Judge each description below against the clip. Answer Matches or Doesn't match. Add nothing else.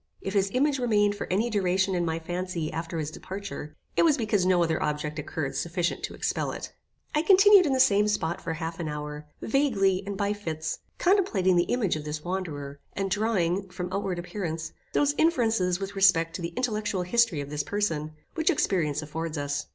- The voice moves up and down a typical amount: Matches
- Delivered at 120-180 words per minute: Doesn't match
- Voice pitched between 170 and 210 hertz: Matches